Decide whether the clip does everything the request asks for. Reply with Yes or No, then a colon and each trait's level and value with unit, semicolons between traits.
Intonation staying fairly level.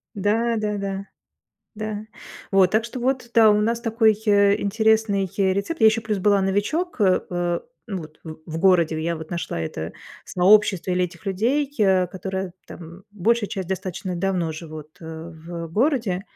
No: average, 3.7 semitones